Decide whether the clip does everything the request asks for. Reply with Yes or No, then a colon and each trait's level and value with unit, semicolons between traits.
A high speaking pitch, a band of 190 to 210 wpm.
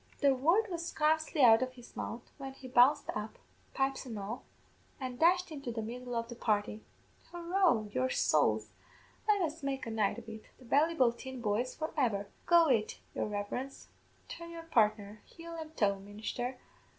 No: very high, 255 Hz; average, 175 wpm